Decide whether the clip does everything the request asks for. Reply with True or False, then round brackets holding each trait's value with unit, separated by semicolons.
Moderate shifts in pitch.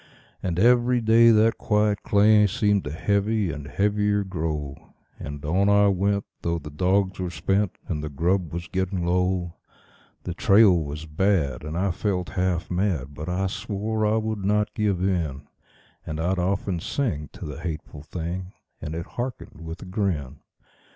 True (4.0 semitones)